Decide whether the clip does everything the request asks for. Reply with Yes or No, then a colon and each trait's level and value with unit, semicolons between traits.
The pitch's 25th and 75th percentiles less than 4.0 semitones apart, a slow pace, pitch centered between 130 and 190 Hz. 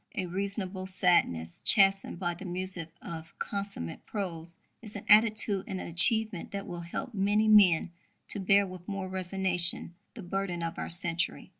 No: narrow, 2.4 semitones; average, 160 wpm; medium, 185 Hz